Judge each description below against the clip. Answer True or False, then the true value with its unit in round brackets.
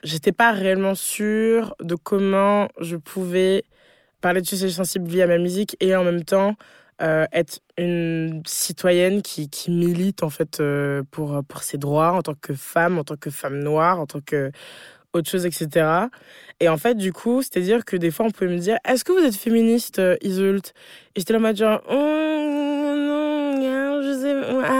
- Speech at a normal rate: True (185 wpm)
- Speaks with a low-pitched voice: False (185 Hz)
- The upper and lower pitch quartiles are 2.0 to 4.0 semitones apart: False (5.3 semitones)